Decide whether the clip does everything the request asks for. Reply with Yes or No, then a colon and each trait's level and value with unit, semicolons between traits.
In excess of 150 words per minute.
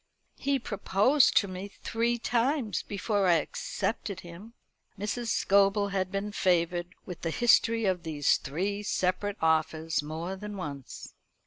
No: slow, 135 wpm